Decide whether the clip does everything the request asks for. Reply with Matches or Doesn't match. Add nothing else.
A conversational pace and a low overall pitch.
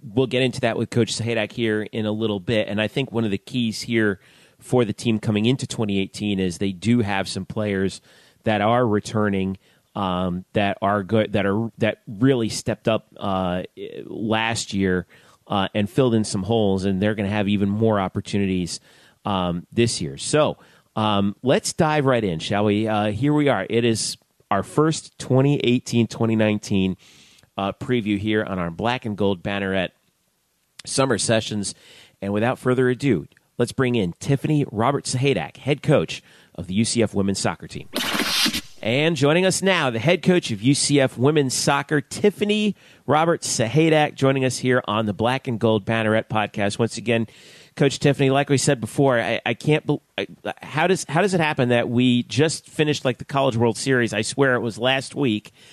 Matches